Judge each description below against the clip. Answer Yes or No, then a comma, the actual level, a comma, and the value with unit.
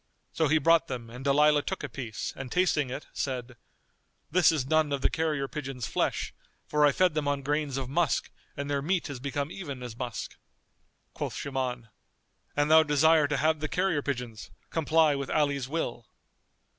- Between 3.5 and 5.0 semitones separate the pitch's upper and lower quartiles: No, average, 2.9 semitones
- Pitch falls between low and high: Yes, medium, 145 Hz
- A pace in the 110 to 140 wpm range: No, average, 180 wpm